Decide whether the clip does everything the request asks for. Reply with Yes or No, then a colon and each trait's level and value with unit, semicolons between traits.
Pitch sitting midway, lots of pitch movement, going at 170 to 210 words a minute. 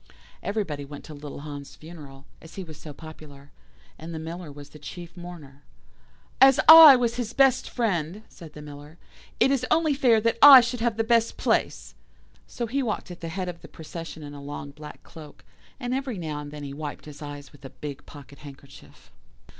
Yes: medium, 160 Hz; wide, 7.8 semitones; average, 200 wpm